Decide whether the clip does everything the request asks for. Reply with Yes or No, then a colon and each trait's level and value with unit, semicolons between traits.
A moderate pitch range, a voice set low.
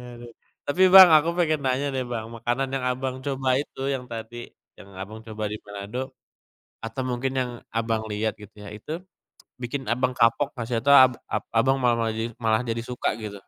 Yes: average, 3.1 semitones; low, 120 Hz